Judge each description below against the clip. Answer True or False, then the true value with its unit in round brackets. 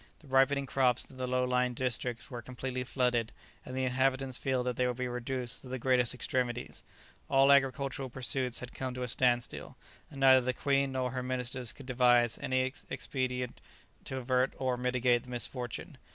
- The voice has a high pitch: False (125 Hz)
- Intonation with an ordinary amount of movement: False (1.0 semitones)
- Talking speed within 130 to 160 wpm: False (180 wpm)